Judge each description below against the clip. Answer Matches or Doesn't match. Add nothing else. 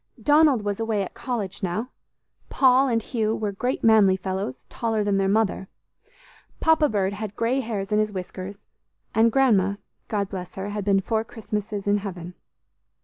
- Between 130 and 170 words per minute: Matches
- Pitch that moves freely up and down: Doesn't match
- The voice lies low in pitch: Doesn't match